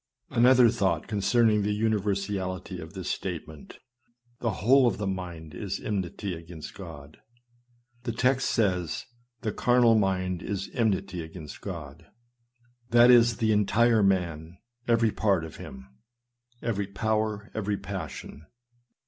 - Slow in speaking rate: Yes, slow, 130 wpm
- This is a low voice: Yes, low, 100 Hz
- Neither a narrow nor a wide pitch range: Yes, average, 4.0 semitones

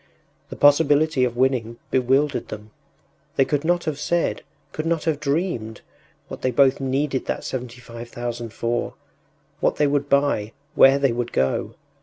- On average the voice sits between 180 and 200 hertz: No, low, 135 Hz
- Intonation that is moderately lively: Yes, average, 3.5 semitones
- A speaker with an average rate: Yes, average, 160 wpm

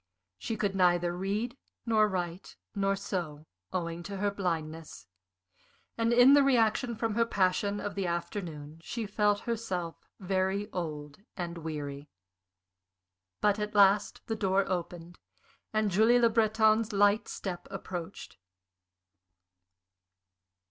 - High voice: Yes, high, 195 Hz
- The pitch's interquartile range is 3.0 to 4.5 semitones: Yes, average, 3.7 semitones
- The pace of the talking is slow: Yes, slow, 120 wpm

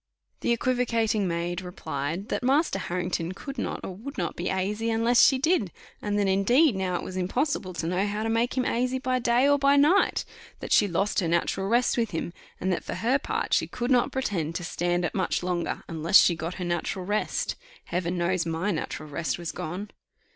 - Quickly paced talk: Yes, fast, 210 wpm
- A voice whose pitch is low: No, high, 195 Hz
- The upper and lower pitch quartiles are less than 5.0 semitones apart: No, wide, 5.5 semitones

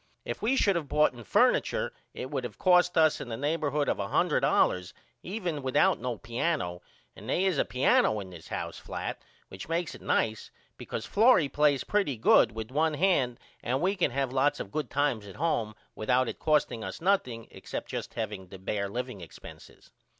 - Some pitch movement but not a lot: No, wide, 6.3 semitones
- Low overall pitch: Yes, low, 130 Hz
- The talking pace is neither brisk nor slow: Yes, average, 180 wpm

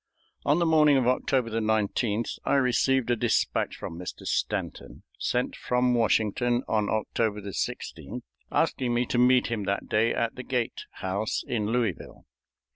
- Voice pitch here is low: Yes, low, 120 Hz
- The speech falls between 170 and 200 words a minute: No, average, 150 wpm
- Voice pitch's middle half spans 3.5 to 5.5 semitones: No, narrow, 2.6 semitones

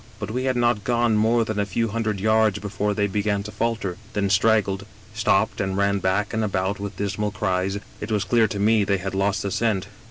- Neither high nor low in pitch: No, low, 105 Hz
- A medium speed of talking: No, fast, 225 wpm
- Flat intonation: Yes, narrow, 1.9 semitones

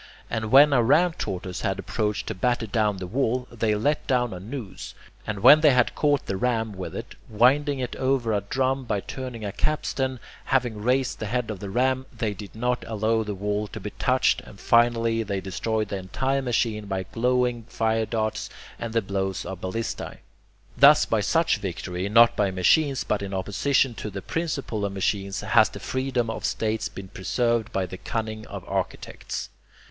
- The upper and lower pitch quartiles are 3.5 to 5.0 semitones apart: Yes, average, 3.9 semitones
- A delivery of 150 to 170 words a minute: No, average, 190 wpm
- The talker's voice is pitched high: No, low, 115 Hz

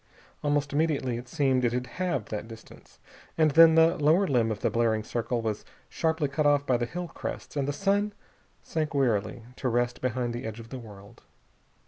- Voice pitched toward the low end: Yes, low, 130 Hz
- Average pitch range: Yes, average, 4.7 semitones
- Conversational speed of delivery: Yes, average, 195 wpm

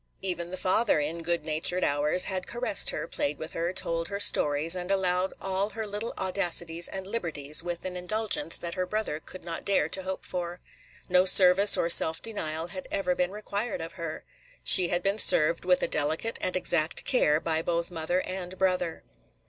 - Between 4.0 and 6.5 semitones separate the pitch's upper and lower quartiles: No, narrow, 2.4 semitones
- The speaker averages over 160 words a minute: Yes, average, 190 wpm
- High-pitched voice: No, medium, 180 Hz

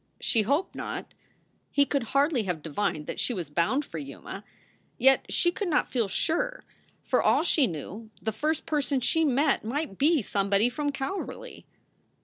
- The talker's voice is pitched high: Yes, very high, 265 Hz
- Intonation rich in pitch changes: Yes, wide, 7.1 semitones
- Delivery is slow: No, average, 165 wpm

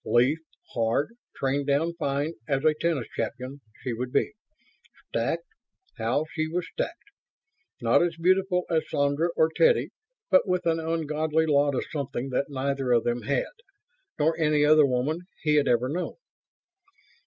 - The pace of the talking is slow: No, average, 155 wpm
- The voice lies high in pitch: No, medium, 150 Hz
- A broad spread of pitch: No, average, 3.4 semitones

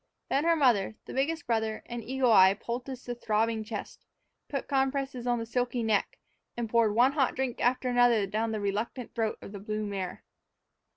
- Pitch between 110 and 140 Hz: No, high, 235 Hz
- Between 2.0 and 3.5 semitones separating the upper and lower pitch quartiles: Yes, average, 2.9 semitones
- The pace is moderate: Yes, average, 185 wpm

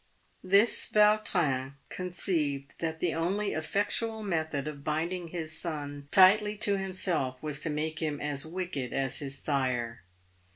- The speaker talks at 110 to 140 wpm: Yes, slow, 135 wpm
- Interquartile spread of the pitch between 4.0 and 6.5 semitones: Yes, average, 4.6 semitones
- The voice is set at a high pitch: No, medium, 160 Hz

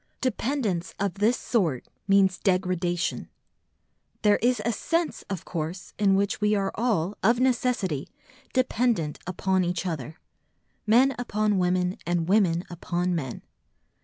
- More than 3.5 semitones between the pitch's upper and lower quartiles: Yes, average, 4.1 semitones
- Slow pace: Yes, slow, 130 wpm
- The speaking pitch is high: Yes, high, 195 Hz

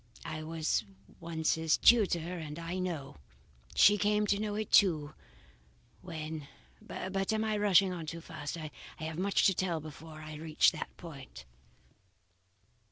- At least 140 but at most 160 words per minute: Yes, average, 150 wpm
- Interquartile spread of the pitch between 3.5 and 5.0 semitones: Yes, average, 3.8 semitones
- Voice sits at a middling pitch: Yes, medium, 165 Hz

